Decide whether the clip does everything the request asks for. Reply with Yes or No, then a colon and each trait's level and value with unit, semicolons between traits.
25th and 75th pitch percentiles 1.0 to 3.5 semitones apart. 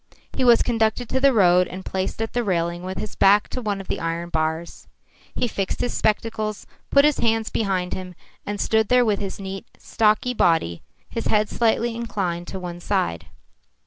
No: average, 4.0 semitones